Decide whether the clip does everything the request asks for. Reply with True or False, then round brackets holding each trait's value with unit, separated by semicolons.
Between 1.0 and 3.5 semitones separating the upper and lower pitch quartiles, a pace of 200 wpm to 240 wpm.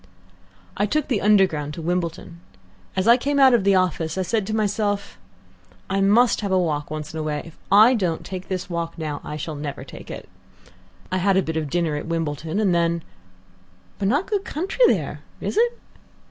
False (4.7 semitones; 205 wpm)